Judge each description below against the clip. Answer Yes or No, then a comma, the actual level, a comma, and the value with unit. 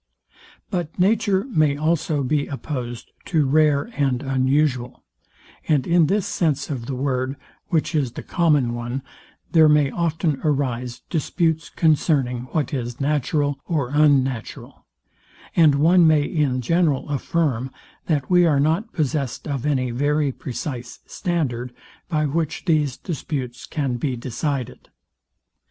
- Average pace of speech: No, slow, 130 wpm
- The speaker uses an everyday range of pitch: Yes, average, 3.6 semitones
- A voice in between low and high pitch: Yes, medium, 145 Hz